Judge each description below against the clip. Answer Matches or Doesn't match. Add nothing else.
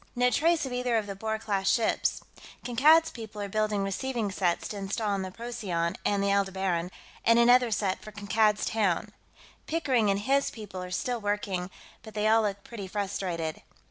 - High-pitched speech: Matches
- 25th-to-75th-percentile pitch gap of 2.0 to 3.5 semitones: Matches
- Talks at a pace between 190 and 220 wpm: Doesn't match